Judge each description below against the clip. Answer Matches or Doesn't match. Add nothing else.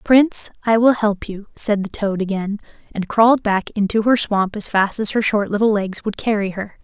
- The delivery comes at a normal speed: Doesn't match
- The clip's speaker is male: Doesn't match